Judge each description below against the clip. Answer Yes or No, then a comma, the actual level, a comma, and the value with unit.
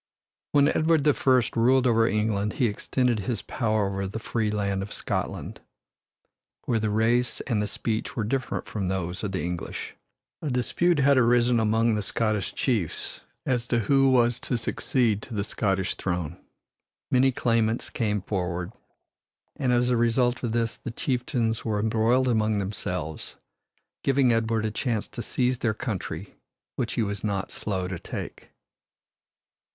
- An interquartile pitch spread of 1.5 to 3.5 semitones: Yes, average, 3.2 semitones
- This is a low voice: Yes, low, 115 Hz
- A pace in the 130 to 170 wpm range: Yes, average, 160 wpm